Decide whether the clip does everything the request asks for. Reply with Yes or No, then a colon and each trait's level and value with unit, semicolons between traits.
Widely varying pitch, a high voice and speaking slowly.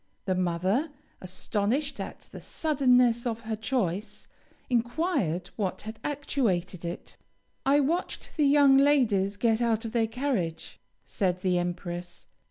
Yes: wide, 6.6 semitones; high, 225 Hz; slow, 130 wpm